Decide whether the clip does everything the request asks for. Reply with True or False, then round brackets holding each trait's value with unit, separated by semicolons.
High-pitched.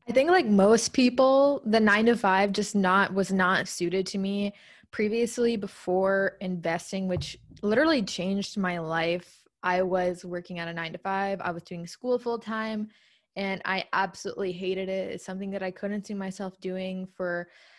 True (195 Hz)